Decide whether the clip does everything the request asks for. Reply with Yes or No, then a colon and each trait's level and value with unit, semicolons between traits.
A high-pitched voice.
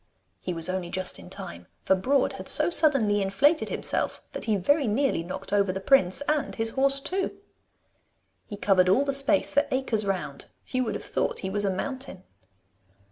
Yes: high, 210 Hz